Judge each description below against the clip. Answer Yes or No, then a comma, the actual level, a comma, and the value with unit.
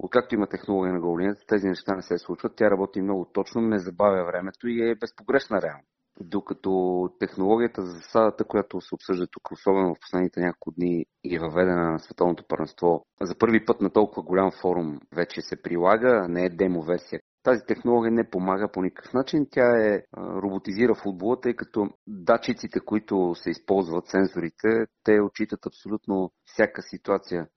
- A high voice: No, low, 100 Hz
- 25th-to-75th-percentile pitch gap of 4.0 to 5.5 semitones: No, average, 3.5 semitones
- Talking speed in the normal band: No, fast, 170 wpm